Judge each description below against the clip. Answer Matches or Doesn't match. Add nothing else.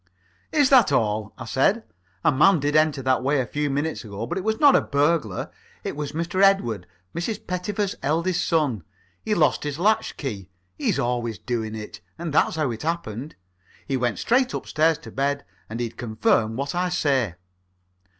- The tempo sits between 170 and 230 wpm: Matches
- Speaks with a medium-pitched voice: Matches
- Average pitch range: Doesn't match